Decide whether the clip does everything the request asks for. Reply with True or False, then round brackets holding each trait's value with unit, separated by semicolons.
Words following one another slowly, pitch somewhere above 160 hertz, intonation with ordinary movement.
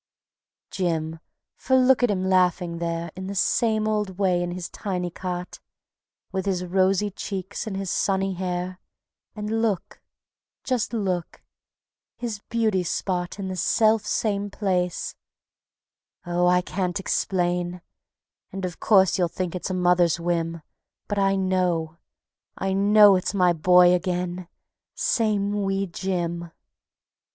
False (130 wpm; 185 Hz; 2.1 semitones)